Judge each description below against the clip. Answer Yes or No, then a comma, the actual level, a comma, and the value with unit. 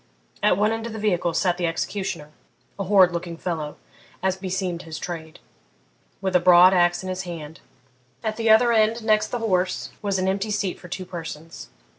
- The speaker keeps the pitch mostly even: No, average, 3.2 semitones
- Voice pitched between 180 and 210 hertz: Yes, medium, 185 Hz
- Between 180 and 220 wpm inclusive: Yes, average, 190 wpm